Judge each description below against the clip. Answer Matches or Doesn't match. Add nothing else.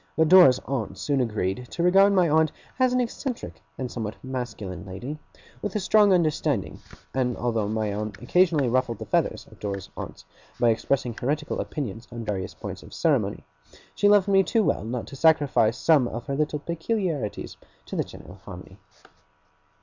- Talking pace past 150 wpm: Matches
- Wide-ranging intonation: Matches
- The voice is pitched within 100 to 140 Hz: Matches